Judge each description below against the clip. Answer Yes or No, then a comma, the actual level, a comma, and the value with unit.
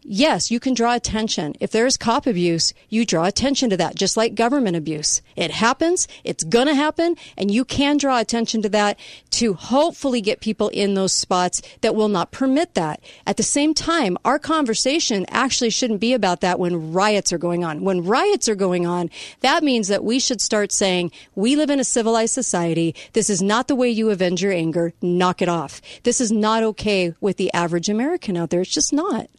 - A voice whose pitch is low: No, high, 220 Hz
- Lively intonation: Yes, wide, 5.9 semitones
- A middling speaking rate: No, fast, 210 wpm